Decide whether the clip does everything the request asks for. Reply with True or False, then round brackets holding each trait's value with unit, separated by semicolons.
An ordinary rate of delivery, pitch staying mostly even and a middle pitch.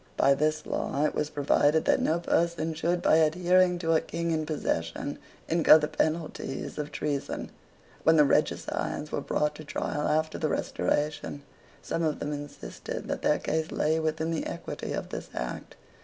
True (170 wpm; 1.6 semitones; 155 Hz)